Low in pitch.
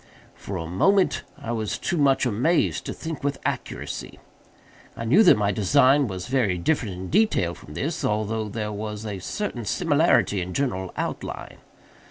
Yes: low, 110 Hz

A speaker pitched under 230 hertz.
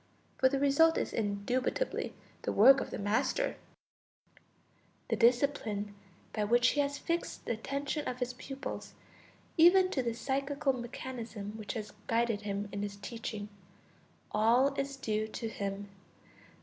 No: high, 240 Hz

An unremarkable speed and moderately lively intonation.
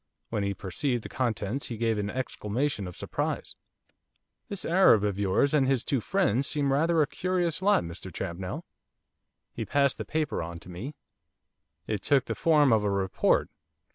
No: average, 170 wpm; wide, 6.7 semitones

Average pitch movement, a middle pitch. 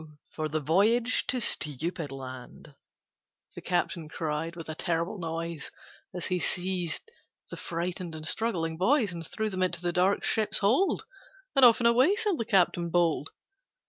Yes: average, 4.6 semitones; medium, 175 Hz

